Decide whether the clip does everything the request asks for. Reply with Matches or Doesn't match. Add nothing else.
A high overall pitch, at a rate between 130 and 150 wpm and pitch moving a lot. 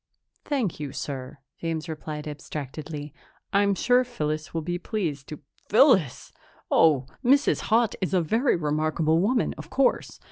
Doesn't match